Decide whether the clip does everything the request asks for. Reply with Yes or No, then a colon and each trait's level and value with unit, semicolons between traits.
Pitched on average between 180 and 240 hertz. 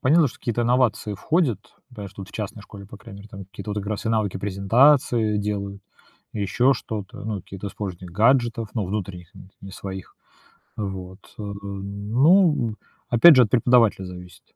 No: low, 105 Hz